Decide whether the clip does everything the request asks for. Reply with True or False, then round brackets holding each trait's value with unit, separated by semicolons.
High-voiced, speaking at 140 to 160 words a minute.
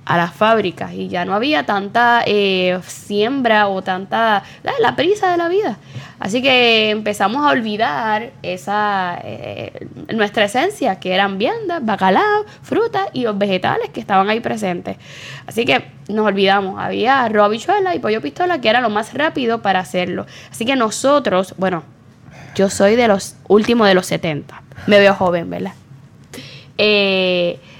True (205 Hz; 155 wpm)